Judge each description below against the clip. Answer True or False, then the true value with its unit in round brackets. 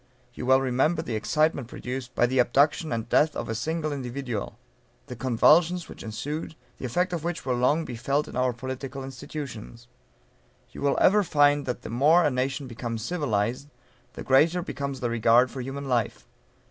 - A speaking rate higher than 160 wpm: True (180 wpm)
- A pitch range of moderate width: True (3.5 semitones)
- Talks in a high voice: False (135 Hz)